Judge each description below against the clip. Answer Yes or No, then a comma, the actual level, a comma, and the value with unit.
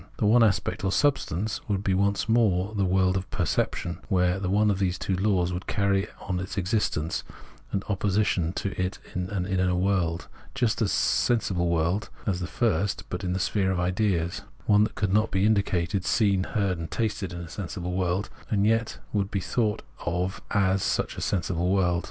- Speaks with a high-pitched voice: No, very low, 95 Hz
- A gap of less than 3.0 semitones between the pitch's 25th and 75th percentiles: Yes, narrow, 2.4 semitones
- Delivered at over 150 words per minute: Yes, average, 195 wpm